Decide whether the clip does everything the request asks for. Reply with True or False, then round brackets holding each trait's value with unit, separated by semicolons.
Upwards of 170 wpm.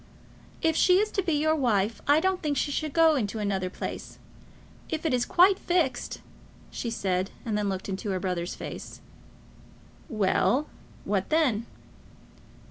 False (165 wpm)